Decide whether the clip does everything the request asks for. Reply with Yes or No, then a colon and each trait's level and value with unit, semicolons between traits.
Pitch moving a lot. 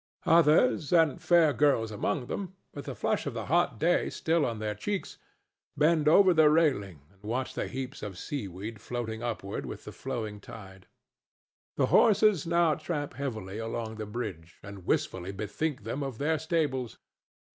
Yes: wide, 6.8 semitones